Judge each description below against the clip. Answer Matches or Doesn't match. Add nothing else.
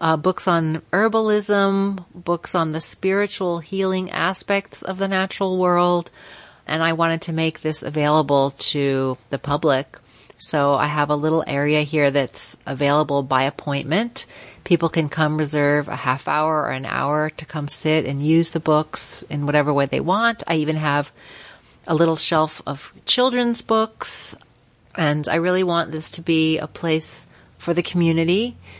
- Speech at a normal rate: Matches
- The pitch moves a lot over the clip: Doesn't match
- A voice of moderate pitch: Matches